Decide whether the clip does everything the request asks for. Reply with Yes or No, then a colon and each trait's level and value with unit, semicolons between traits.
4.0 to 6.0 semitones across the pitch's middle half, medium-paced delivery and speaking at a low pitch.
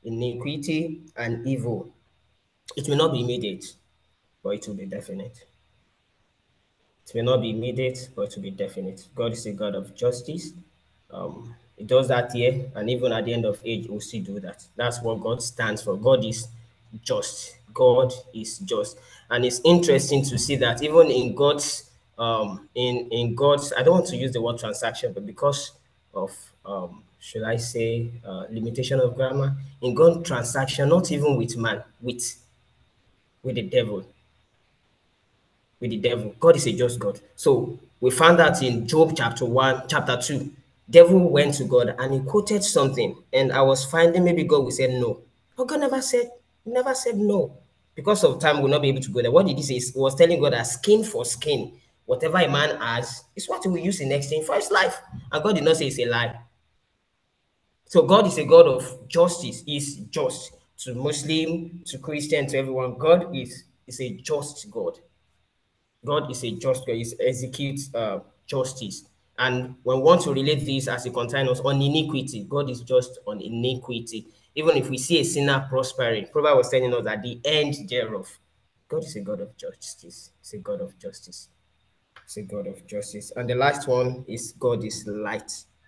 Yes: average, 4.7 semitones; average, 190 wpm; low, 130 Hz